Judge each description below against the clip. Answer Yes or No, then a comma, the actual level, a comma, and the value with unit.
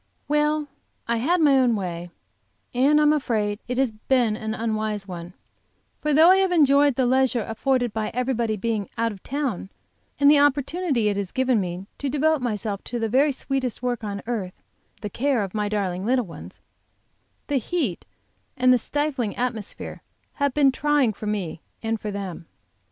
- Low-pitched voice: No, high, 240 Hz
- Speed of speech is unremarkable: Yes, average, 180 wpm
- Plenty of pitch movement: No, average, 5.0 semitones